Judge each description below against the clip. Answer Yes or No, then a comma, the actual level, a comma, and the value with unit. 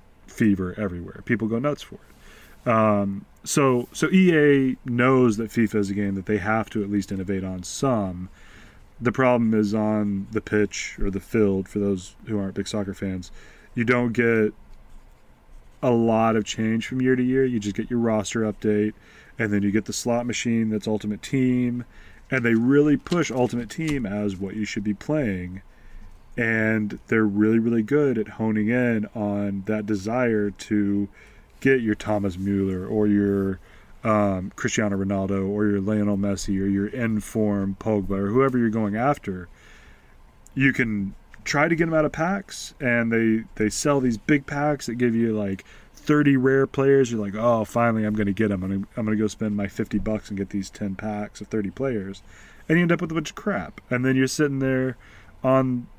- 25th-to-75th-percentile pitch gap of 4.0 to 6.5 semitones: No, average, 3.5 semitones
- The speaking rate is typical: Yes, average, 190 wpm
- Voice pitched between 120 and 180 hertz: No, low, 110 Hz